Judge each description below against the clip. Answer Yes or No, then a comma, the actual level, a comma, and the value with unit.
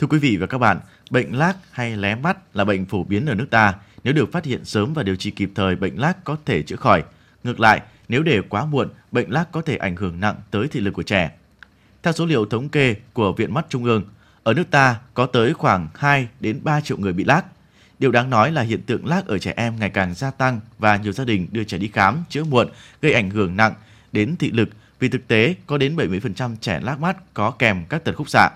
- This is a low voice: Yes, low, 115 Hz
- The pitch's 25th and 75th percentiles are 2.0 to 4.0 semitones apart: No, average, 5.1 semitones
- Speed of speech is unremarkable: No, fast, 255 wpm